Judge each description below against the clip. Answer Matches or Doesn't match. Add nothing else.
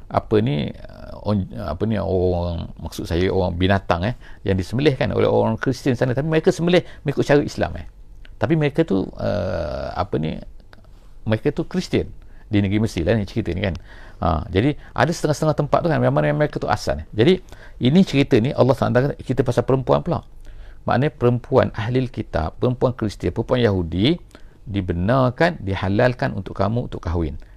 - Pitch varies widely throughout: Matches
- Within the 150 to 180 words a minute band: Matches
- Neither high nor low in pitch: Doesn't match